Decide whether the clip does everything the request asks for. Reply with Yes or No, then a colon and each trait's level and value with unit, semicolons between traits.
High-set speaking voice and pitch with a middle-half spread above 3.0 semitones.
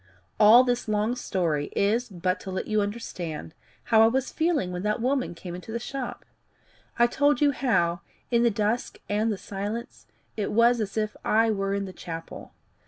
Yes: high, 215 Hz; average, 3.6 semitones